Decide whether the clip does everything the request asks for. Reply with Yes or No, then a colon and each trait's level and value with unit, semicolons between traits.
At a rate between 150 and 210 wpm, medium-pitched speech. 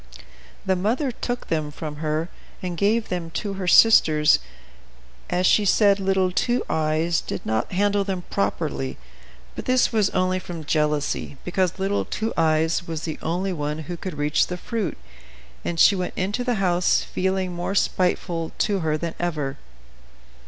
Yes: average, 160 wpm; medium, 180 Hz